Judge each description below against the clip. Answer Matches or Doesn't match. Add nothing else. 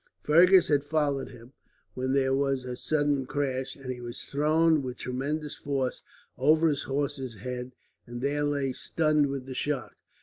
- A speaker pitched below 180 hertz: Matches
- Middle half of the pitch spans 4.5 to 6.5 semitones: Doesn't match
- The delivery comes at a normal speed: Matches